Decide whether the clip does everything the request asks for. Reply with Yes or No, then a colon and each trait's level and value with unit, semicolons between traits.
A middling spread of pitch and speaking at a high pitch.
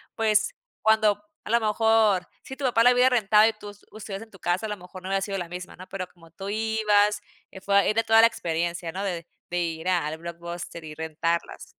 Yes: average, 4.1 semitones; high, 195 Hz